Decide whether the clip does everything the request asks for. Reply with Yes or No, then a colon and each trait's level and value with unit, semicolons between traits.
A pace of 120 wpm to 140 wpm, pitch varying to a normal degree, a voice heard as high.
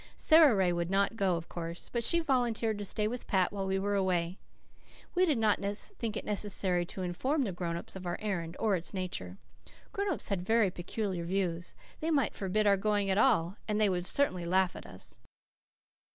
No: fast, 205 wpm; average, 3.7 semitones; high, 195 Hz